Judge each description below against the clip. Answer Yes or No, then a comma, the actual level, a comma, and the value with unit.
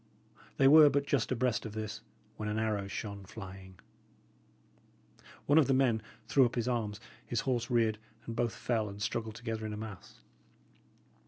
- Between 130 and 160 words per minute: No, average, 170 wpm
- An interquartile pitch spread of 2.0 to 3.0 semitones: Yes, average, 2.7 semitones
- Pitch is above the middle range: No, low, 110 Hz